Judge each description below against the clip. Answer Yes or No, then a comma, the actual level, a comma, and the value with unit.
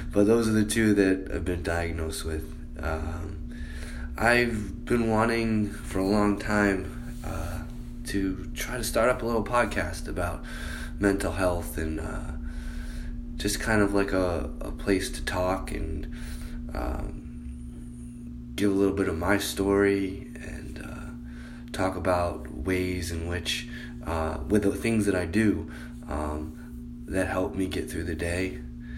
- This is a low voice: Yes, very low, 80 Hz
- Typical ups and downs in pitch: No, wide, 8.4 semitones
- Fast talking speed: No, average, 150 wpm